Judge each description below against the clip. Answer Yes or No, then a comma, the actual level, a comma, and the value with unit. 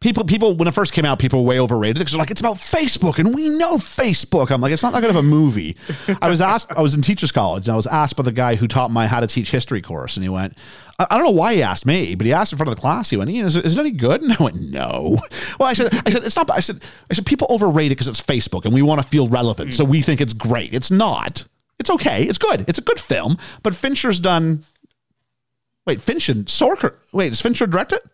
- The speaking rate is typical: No, fast, 280 wpm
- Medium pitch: Yes, medium, 160 Hz